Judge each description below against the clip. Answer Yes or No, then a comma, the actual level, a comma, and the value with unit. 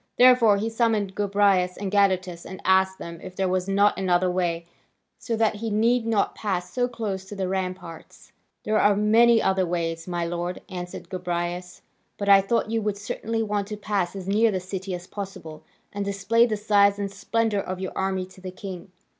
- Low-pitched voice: No, high, 195 Hz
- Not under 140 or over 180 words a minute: No, average, 195 wpm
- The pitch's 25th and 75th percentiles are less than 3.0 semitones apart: Yes, narrow, 2.4 semitones